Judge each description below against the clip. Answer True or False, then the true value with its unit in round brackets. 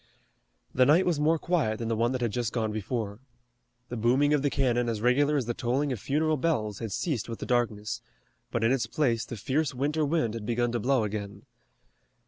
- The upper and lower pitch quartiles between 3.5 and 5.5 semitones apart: True (4.3 semitones)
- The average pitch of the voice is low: True (120 Hz)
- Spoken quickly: True (215 wpm)